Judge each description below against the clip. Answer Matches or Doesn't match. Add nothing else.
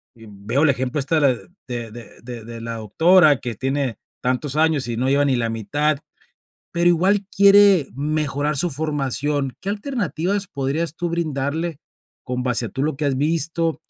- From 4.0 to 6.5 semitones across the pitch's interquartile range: Matches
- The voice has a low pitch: Doesn't match